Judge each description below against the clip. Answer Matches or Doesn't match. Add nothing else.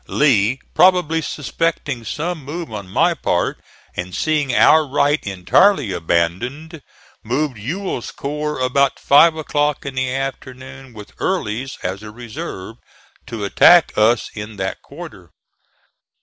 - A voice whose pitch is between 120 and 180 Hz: Matches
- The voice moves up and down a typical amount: Doesn't match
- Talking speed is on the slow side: Matches